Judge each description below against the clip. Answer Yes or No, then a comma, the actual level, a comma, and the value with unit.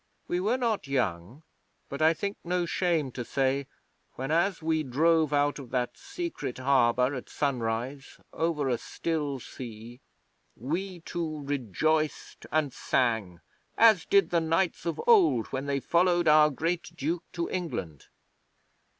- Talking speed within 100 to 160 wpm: Yes, average, 140 wpm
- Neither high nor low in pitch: Yes, medium, 150 Hz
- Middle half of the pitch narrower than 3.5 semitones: No, average, 4.7 semitones